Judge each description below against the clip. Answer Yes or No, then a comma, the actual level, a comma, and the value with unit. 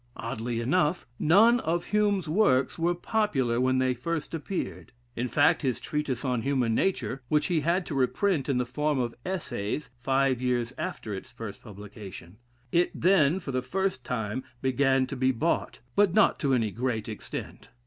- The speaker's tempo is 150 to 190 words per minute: Yes, average, 170 wpm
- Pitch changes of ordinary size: No, wide, 5.8 semitones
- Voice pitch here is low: Yes, low, 130 Hz